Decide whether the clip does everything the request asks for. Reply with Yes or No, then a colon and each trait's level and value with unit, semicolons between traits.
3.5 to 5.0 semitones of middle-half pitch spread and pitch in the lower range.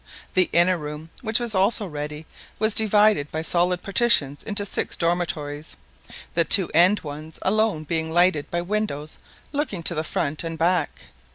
No: average, 4.6 semitones; medium, 175 Hz